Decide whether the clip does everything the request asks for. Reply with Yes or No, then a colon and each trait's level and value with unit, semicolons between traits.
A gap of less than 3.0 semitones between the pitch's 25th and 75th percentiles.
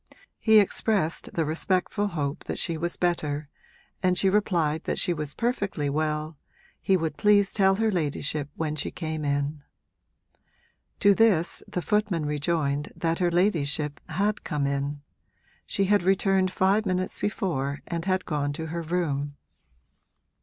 No: average, 4.5 semitones